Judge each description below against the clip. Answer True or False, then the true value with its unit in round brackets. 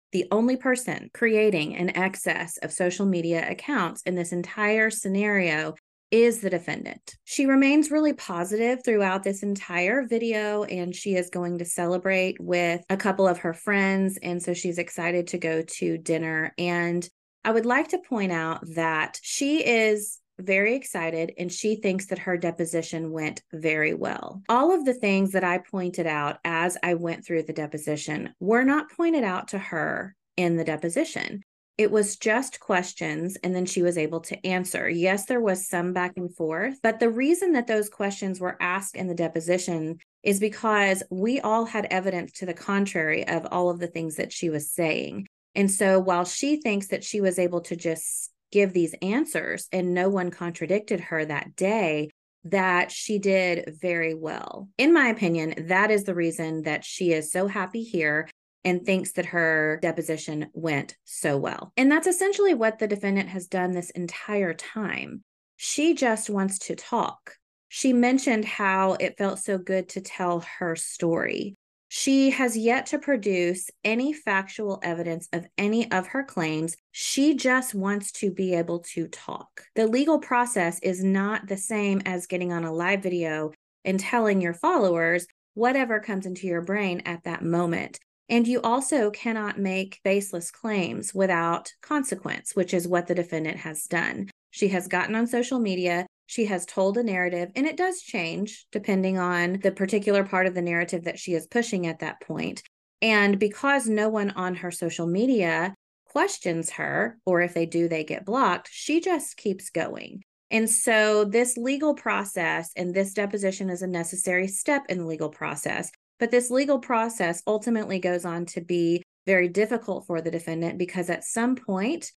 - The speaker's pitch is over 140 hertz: True (190 Hz)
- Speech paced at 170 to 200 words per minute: True (175 wpm)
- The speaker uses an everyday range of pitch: True (3.9 semitones)